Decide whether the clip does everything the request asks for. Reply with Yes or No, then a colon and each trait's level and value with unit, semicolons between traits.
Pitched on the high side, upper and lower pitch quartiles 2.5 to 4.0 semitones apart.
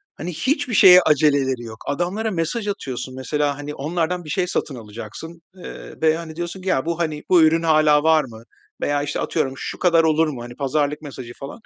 No: medium, 155 Hz; average, 3.5 semitones